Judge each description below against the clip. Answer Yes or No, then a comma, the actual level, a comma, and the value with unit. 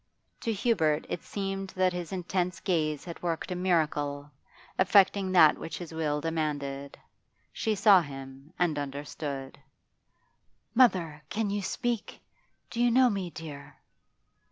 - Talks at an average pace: No, slow, 130 wpm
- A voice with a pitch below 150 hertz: No, medium, 175 Hz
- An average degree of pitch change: Yes, average, 4.6 semitones